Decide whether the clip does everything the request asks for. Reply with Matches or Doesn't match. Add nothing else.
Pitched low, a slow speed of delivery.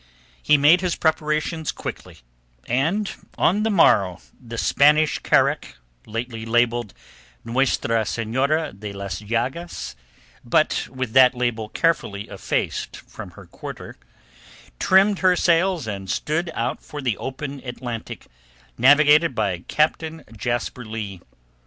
Matches